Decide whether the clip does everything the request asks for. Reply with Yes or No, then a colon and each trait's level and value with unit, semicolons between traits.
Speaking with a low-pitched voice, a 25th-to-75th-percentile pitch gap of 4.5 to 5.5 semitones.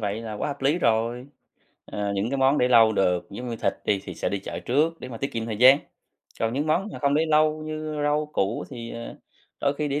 Yes: low, 125 Hz; average, 5.0 semitones